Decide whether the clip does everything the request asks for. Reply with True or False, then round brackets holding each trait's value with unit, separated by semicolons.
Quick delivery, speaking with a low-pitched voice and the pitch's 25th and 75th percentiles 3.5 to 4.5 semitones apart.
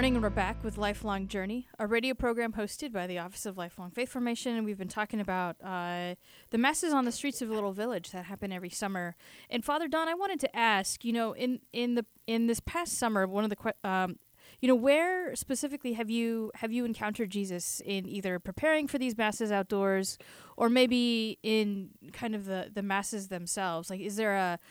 False (210 wpm; 215 Hz; 3.9 semitones)